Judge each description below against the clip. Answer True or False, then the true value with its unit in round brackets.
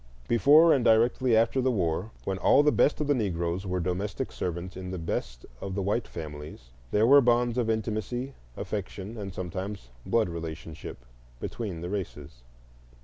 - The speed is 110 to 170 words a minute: True (165 wpm)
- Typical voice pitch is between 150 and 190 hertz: False (100 Hz)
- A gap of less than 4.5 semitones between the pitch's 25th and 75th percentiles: False (5.3 semitones)